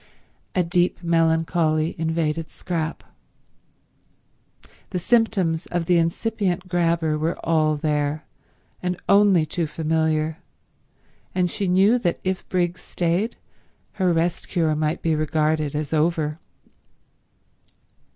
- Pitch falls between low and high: Yes, medium, 165 Hz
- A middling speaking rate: No, slow, 110 wpm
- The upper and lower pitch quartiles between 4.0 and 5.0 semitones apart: No, narrow, 2.4 semitones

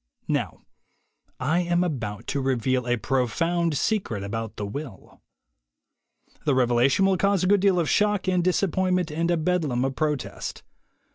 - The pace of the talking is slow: No, average, 150 wpm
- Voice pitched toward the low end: No, medium, 155 Hz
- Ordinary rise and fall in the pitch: No, wide, 6.2 semitones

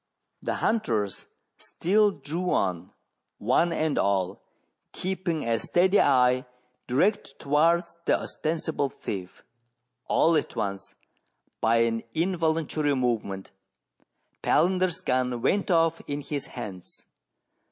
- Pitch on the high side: No, medium, 145 Hz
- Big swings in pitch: Yes, wide, 6.5 semitones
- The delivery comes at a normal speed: No, slow, 105 wpm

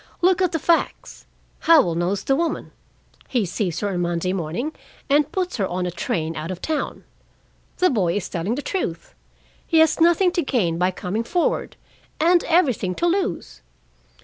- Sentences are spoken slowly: No, average, 175 wpm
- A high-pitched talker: Yes, high, 230 Hz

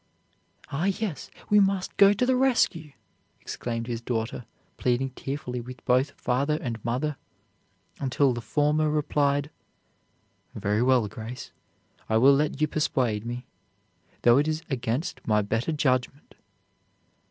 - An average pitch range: Yes, average, 4.1 semitones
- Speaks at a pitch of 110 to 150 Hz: Yes, low, 135 Hz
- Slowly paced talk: Yes, slow, 130 wpm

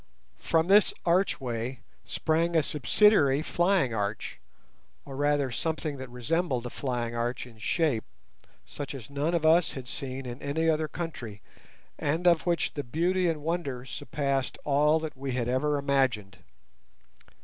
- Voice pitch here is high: No, medium, 140 Hz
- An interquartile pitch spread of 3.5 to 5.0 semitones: Yes, average, 4.4 semitones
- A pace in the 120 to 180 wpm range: Yes, average, 150 wpm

